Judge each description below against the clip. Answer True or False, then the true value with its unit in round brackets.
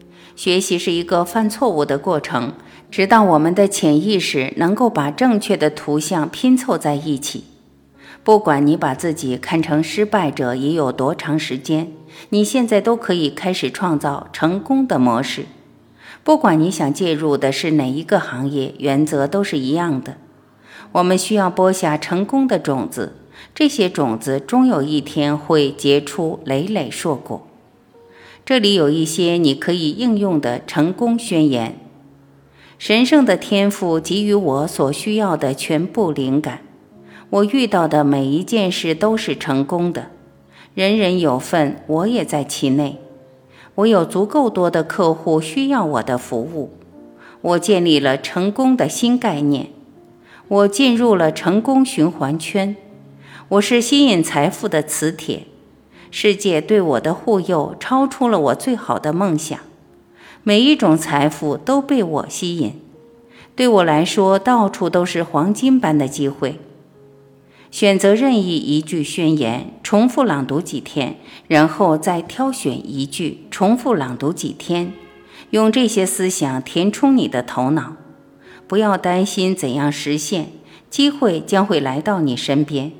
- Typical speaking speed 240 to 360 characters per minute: False (215 characters per minute)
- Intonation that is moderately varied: False (6.1 semitones)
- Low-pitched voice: False (165 Hz)